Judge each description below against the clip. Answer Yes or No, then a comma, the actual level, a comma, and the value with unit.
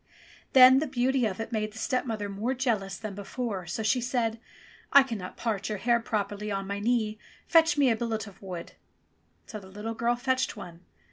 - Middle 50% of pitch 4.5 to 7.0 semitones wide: No, average, 3.4 semitones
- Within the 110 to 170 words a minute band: No, average, 195 wpm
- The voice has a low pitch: No, high, 225 Hz